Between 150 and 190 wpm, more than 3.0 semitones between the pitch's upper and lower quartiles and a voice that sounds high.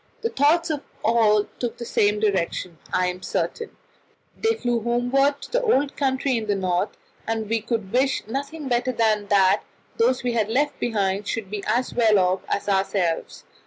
Yes: average, 180 wpm; average, 4.6 semitones; high, 225 Hz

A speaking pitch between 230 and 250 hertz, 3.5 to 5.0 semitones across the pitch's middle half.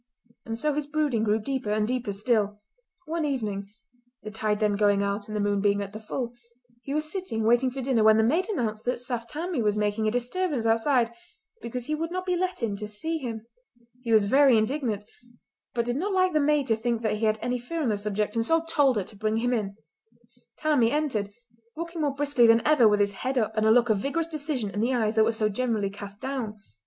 Yes: high, 235 Hz; average, 4.6 semitones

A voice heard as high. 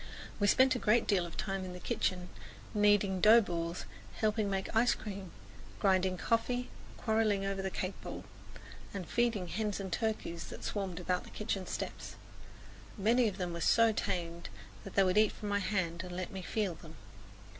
Yes: high, 195 Hz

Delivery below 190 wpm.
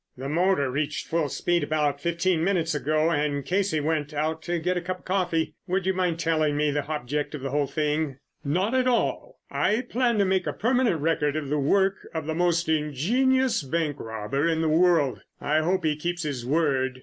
No: fast, 205 wpm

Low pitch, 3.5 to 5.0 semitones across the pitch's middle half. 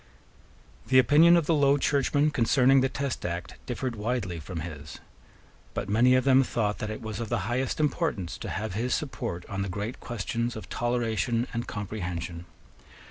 Yes: low, 115 Hz; average, 4.5 semitones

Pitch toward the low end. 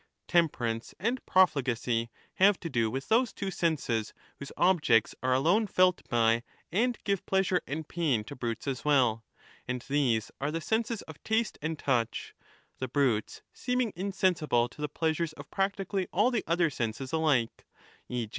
No: medium, 155 Hz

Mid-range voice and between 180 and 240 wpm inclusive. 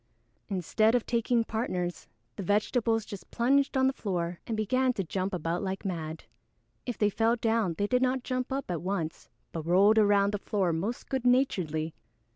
No: high, 210 Hz; average, 190 wpm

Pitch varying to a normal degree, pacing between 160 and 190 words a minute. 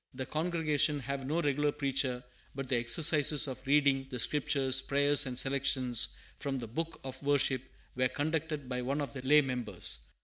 No: narrow, 2.2 semitones; average, 170 wpm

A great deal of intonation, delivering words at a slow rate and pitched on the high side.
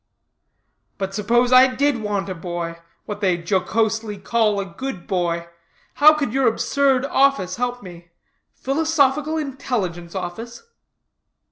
Yes: wide, 6.3 semitones; slow, 125 wpm; high, 220 Hz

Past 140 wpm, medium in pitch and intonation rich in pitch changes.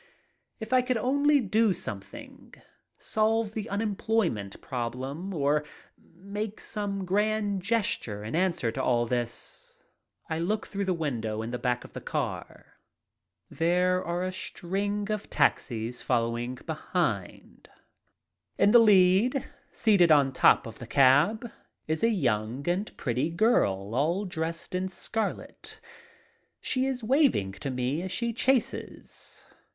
No: slow, 135 wpm; medium, 180 Hz; wide, 9.0 semitones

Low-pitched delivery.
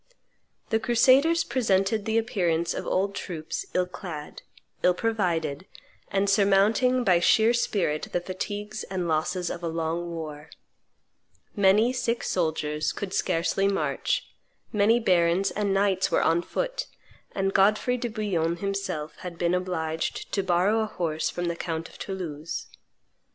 No: high, 190 Hz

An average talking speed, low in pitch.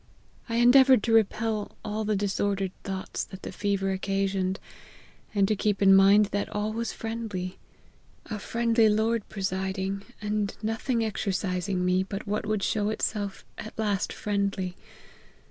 No: average, 145 wpm; high, 205 Hz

